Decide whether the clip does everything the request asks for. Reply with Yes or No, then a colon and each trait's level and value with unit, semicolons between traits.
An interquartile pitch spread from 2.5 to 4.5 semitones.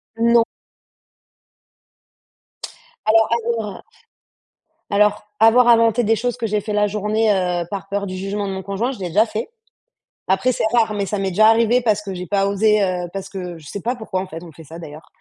Yes: average, 2.8 semitones